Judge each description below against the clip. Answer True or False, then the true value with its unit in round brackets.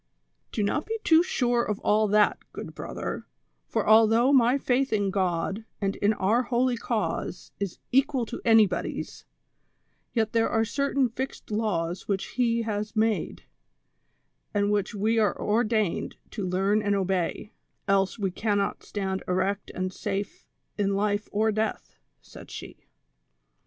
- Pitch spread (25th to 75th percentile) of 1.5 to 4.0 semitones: True (2.8 semitones)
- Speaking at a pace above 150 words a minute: False (145 wpm)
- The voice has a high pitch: True (210 Hz)